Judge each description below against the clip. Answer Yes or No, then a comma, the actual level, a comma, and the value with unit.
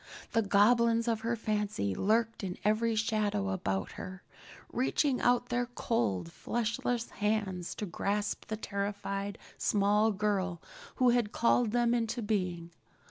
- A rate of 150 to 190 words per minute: No, slow, 135 wpm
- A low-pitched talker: No, high, 210 Hz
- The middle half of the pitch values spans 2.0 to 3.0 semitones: Yes, average, 2.7 semitones